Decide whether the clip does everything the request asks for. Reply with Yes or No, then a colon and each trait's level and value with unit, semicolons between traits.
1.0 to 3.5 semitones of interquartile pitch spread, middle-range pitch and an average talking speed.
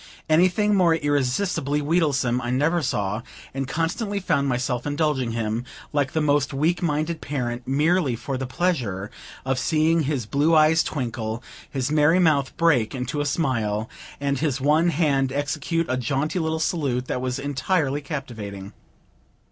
No: average, 4.1 semitones; medium, 145 Hz; average, 150 wpm